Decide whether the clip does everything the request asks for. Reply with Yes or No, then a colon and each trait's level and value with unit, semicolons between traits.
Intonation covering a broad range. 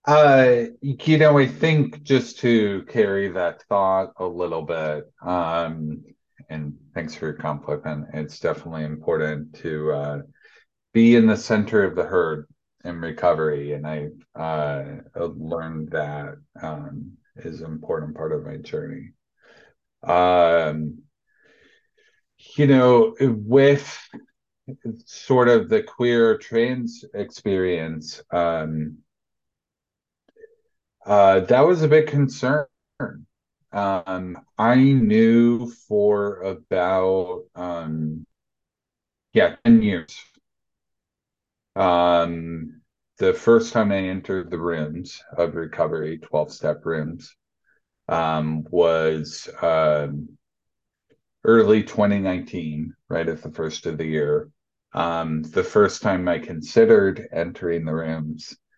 Yes: wide, 7.6 semitones